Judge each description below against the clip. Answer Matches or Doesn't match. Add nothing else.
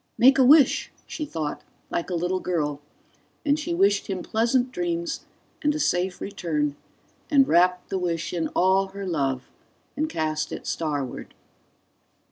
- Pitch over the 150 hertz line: Matches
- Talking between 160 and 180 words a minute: Doesn't match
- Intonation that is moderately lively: Doesn't match